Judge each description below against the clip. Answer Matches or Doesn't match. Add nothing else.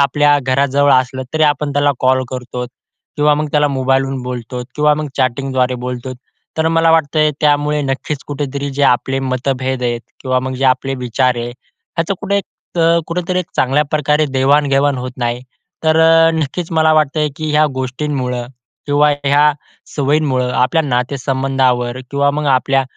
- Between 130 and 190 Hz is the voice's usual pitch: Matches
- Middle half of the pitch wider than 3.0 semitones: Doesn't match